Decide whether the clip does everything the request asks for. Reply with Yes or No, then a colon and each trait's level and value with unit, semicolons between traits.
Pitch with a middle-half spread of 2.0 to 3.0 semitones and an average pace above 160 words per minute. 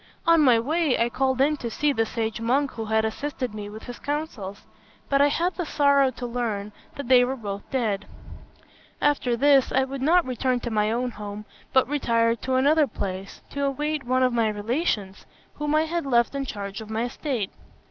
No: average, 4.3 semitones; average, 200 wpm